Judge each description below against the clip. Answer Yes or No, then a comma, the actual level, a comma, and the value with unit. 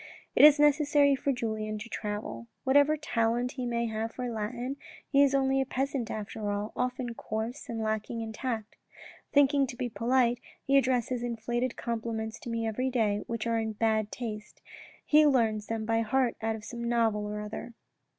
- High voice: Yes, high, 235 Hz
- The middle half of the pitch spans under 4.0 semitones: Yes, average, 3.0 semitones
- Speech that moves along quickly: No, average, 180 wpm